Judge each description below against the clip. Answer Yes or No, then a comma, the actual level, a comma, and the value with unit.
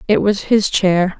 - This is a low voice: No, high, 195 Hz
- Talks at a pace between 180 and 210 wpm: Yes, average, 200 wpm